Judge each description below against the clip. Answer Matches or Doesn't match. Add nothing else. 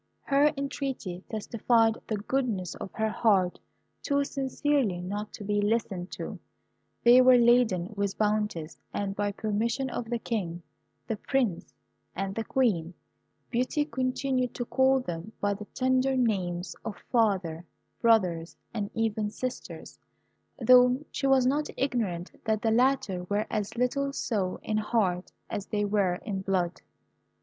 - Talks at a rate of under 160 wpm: Matches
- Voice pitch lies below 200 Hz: Doesn't match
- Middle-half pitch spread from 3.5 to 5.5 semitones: Matches